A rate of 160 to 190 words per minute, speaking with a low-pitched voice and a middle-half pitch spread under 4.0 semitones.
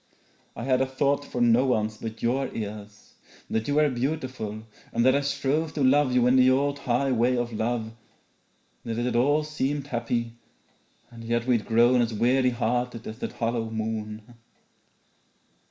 Yes: average, 170 wpm; low, 120 Hz; average, 2.7 semitones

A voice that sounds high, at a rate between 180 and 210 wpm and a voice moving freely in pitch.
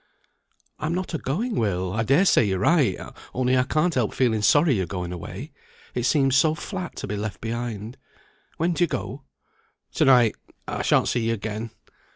No: low, 125 Hz; average, 190 wpm; wide, 6.3 semitones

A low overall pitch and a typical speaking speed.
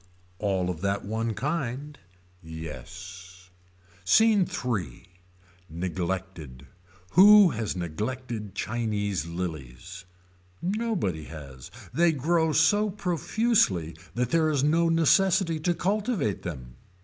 No: low, 110 Hz; slow, 100 wpm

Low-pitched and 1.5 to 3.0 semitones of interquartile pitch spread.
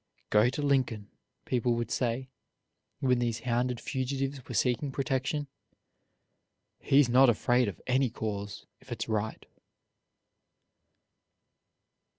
Yes: low, 125 Hz; narrow, 2.6 semitones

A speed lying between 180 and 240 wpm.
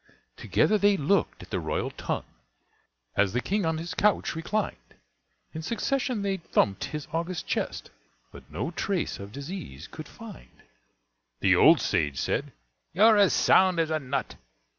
No: average, 155 wpm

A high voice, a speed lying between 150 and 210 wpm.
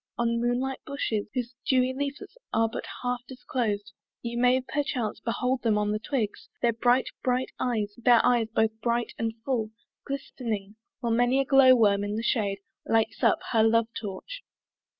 Yes: high, 235 Hz; average, 170 wpm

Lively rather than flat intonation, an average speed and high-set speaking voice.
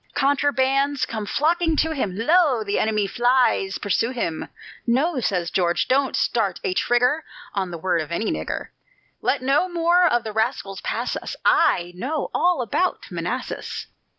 Yes: wide, 6.3 semitones; average, 155 wpm; high, 245 Hz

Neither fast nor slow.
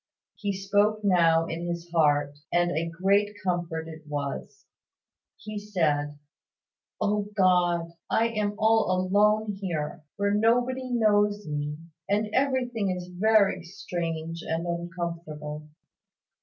No: slow, 115 wpm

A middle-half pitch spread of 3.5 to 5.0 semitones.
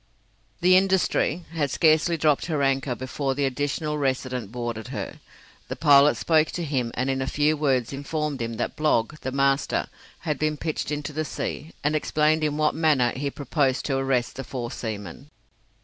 No: average, 2.8 semitones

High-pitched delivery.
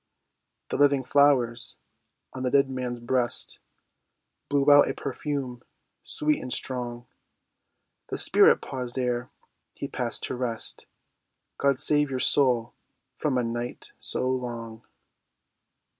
No: low, 130 Hz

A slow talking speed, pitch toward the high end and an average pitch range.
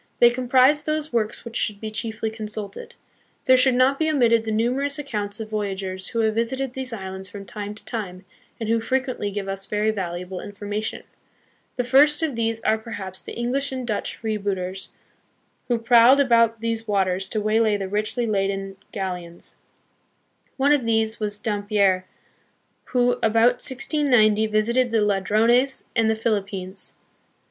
No: average, 155 wpm; high, 220 Hz; average, 3.3 semitones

